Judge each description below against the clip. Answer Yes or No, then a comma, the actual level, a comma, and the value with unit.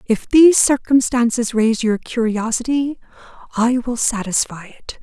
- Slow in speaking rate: Yes, slow, 120 wpm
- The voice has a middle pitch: No, high, 235 Hz